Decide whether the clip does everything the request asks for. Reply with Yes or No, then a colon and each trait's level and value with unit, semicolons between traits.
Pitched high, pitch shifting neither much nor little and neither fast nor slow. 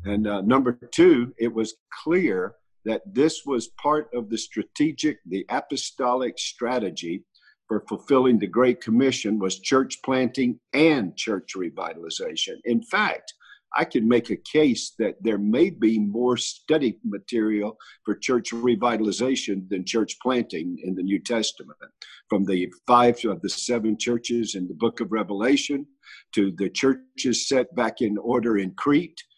No: low, 120 Hz; average, 3.5 semitones; average, 150 wpm